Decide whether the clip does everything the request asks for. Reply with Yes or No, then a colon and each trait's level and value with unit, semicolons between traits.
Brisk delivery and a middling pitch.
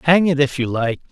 Yes: fast, 270 wpm; medium, 145 Hz